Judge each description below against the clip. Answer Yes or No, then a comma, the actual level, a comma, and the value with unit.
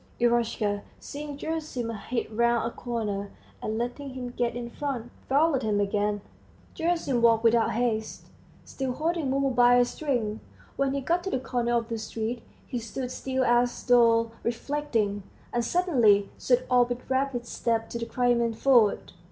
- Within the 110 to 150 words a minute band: No, average, 160 wpm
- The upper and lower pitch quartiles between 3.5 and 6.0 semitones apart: No, narrow, 2.6 semitones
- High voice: Yes, high, 240 Hz